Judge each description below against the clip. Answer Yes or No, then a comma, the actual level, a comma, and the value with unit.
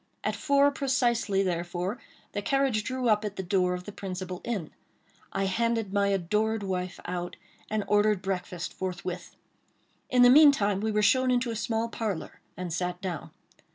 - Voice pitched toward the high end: Yes, high, 205 Hz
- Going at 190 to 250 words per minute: No, average, 165 wpm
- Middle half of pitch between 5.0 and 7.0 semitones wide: No, average, 4.1 semitones